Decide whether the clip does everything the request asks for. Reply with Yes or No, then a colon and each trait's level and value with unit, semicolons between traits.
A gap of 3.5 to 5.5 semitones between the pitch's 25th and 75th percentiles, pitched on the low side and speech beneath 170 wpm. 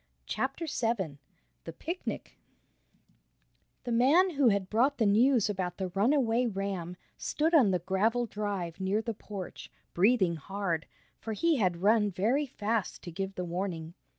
No: average, 4.6 semitones; high, 205 Hz; average, 150 wpm